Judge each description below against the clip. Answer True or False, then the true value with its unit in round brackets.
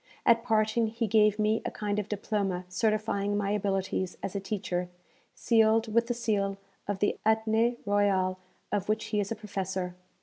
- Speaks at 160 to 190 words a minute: True (170 wpm)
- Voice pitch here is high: True (210 Hz)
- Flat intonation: True (2.0 semitones)